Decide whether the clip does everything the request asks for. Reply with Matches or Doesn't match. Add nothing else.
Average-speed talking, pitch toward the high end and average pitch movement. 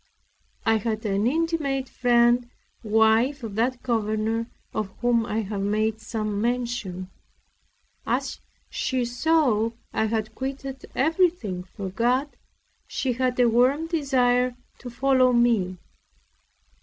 Doesn't match